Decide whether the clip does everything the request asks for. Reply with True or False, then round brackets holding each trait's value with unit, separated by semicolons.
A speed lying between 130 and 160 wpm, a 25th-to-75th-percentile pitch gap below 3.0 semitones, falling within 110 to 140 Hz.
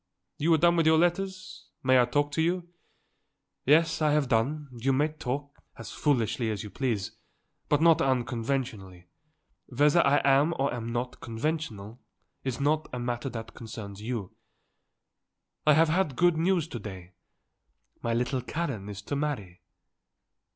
False (155 wpm; 5.1 semitones; 135 Hz)